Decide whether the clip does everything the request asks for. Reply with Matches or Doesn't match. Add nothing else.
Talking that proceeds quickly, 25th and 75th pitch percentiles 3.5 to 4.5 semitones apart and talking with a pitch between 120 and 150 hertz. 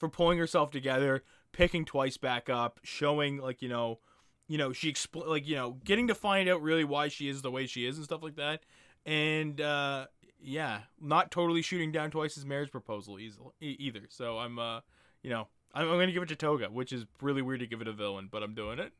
Matches